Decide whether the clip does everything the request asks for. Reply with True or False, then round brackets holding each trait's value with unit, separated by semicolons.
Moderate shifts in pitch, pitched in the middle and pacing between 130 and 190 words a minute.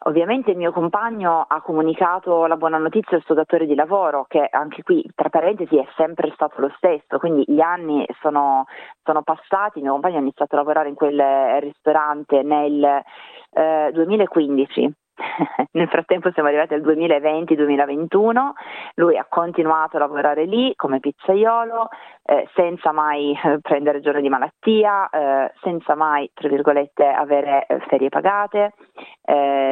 True (3.2 semitones; 155 Hz; 150 wpm)